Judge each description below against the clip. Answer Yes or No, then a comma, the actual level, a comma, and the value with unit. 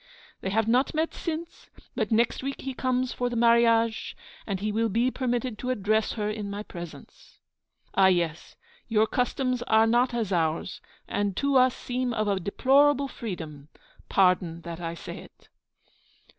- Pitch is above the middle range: Yes, high, 225 Hz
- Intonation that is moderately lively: Yes, average, 4.6 semitones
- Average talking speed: Yes, average, 165 wpm